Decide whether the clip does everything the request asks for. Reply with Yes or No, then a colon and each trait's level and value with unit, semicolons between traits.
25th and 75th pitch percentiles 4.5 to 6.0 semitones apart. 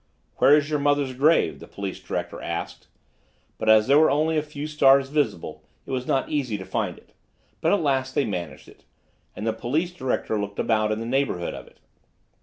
Yes: average, 5.1 semitones